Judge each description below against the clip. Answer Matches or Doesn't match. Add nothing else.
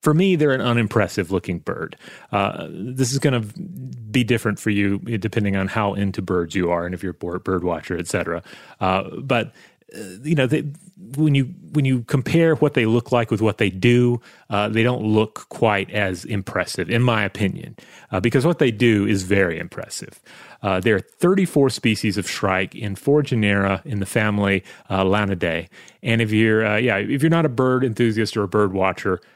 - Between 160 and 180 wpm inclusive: Doesn't match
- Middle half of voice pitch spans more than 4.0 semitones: Matches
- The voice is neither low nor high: Doesn't match